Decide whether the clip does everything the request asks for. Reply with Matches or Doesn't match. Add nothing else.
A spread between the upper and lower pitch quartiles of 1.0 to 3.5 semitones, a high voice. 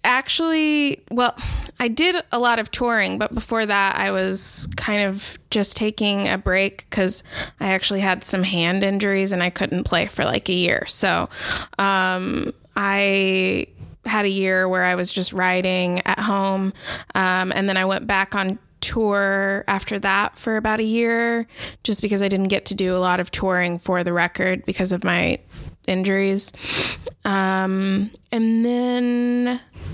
Matches